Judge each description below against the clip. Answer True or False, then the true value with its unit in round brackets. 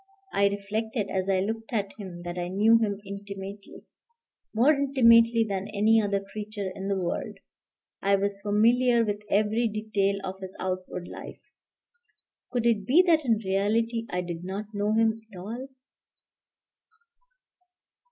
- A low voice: False (205 Hz)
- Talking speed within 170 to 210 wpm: False (145 wpm)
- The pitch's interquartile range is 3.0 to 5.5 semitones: False (2.5 semitones)